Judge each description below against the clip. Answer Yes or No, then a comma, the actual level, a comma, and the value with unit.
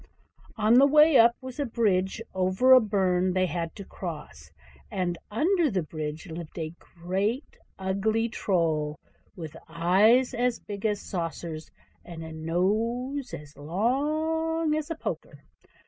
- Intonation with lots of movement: Yes, wide, 6.7 semitones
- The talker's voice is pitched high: Yes, high, 195 Hz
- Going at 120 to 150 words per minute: Yes, average, 140 wpm